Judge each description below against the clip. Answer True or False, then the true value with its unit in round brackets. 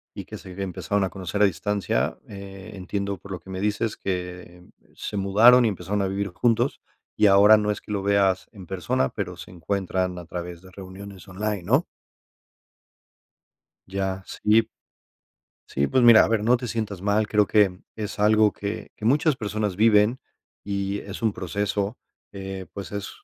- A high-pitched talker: False (100 Hz)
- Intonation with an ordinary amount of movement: False (2.0 semitones)